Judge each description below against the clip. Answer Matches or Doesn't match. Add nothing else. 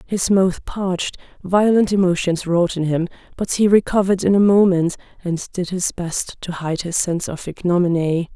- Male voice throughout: Doesn't match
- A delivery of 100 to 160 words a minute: Doesn't match